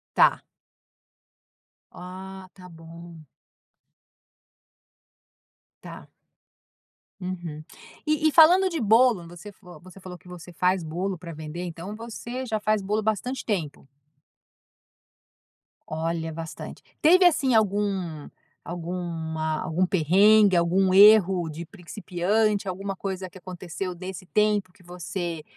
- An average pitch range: Yes, average, 3.5 semitones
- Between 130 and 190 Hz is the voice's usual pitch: Yes, medium, 185 Hz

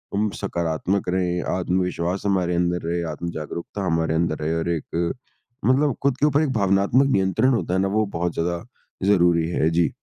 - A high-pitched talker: No, very low, 90 Hz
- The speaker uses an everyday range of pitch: Yes, average, 3.0 semitones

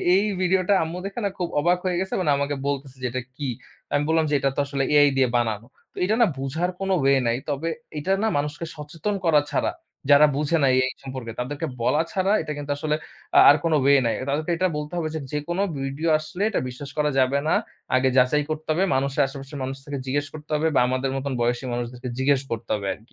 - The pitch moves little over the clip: No, average, 3.2 semitones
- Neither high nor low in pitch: Yes, medium, 145 Hz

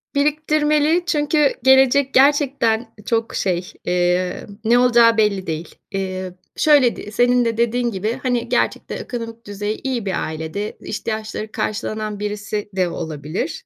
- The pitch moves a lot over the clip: No, average, 4.4 semitones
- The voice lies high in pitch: Yes, high, 225 Hz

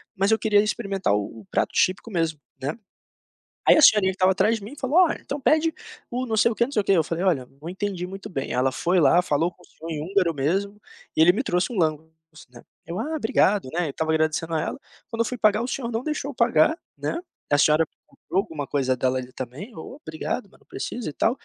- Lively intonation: Yes, wide, 6.2 semitones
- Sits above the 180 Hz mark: Yes, high, 190 Hz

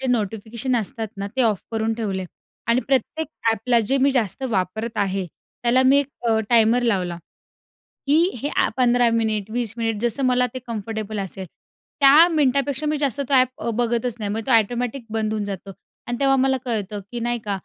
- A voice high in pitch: Yes, high, 235 Hz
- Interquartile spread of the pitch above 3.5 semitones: No, average, 3.1 semitones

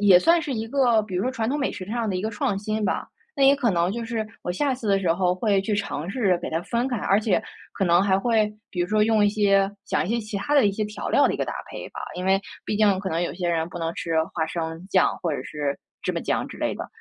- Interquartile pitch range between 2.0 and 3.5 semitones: No, average, 3.9 semitones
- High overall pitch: Yes, high, 200 Hz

